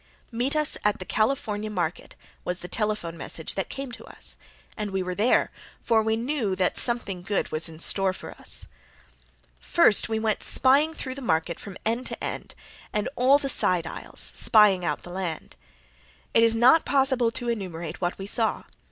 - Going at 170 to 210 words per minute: Yes, average, 180 wpm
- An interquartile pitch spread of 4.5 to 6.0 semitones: Yes, average, 4.8 semitones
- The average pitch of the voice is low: No, high, 210 Hz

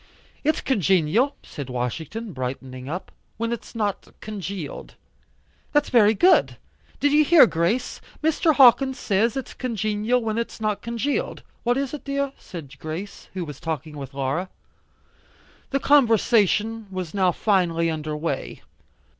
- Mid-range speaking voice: No, high, 210 Hz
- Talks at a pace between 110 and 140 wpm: Yes, slow, 135 wpm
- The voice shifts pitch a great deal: Yes, wide, 7.0 semitones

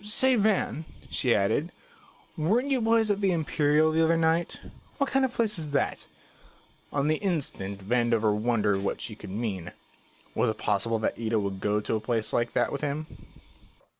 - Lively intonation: Yes, wide, 8.6 semitones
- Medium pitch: Yes, medium, 145 Hz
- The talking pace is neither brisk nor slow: Yes, average, 185 wpm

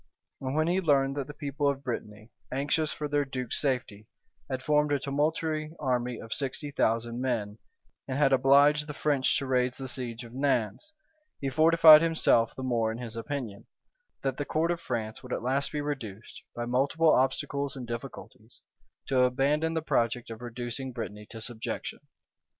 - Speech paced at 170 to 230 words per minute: Yes, average, 175 wpm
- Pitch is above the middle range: No, low, 135 Hz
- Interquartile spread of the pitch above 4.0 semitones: No, average, 3.6 semitones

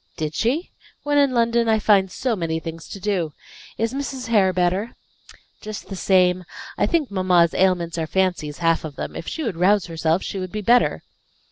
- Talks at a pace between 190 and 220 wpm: Yes, average, 195 wpm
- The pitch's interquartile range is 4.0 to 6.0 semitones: Yes, average, 5.1 semitones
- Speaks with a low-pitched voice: No, high, 190 Hz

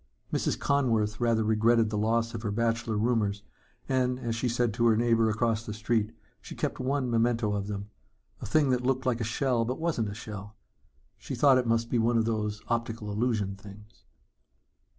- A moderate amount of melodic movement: No, narrow, 2.1 semitones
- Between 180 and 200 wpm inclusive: Yes, average, 190 wpm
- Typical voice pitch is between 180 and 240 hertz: No, low, 115 Hz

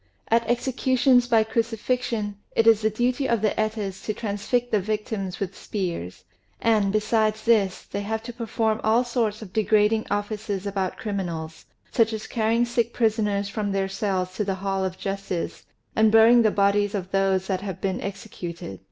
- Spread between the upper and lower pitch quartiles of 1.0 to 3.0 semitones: Yes, narrow, 2.4 semitones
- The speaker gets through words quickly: No, average, 170 wpm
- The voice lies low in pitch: No, high, 215 Hz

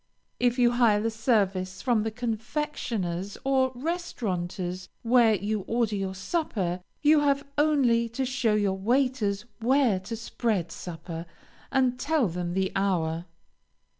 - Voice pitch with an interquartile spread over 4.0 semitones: Yes, average, 5.0 semitones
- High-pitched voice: Yes, high, 225 Hz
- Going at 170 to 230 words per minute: No, slow, 135 wpm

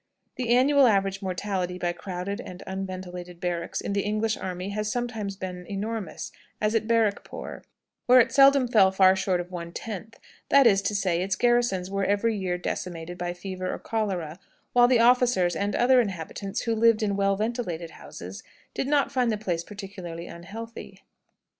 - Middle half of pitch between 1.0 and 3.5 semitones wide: No, average, 4.0 semitones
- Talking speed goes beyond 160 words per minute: Yes, average, 170 wpm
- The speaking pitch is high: Yes, high, 200 Hz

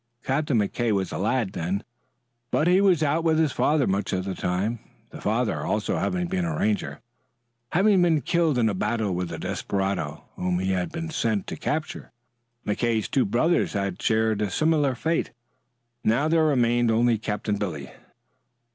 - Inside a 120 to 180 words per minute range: Yes, average, 175 wpm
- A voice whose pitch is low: Yes, low, 120 Hz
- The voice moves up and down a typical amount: No, wide, 7.8 semitones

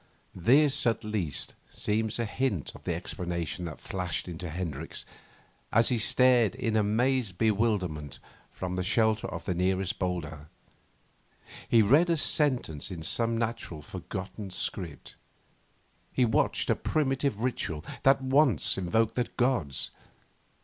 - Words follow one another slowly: Yes, slow, 130 wpm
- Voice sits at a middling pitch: No, low, 105 Hz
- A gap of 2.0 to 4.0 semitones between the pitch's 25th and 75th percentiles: No, wide, 5.5 semitones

